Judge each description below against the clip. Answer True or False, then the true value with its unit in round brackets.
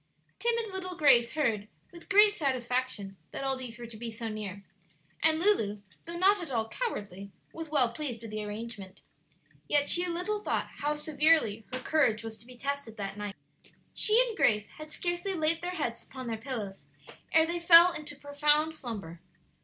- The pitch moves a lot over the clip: True (6.9 semitones)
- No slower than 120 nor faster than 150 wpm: False (180 wpm)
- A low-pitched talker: False (275 Hz)